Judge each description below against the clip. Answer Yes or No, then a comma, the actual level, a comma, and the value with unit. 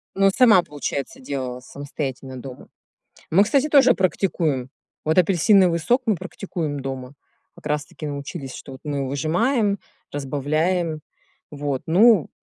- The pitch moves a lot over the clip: Yes, wide, 5.8 semitones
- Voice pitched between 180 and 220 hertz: No, medium, 155 Hz